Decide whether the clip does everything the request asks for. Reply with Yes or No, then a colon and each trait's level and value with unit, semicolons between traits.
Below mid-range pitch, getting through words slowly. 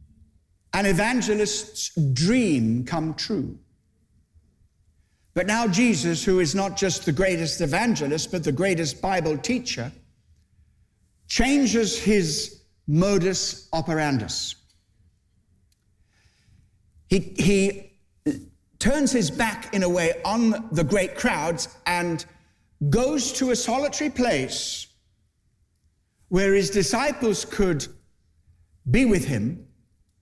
No: medium, 165 Hz; slow, 95 wpm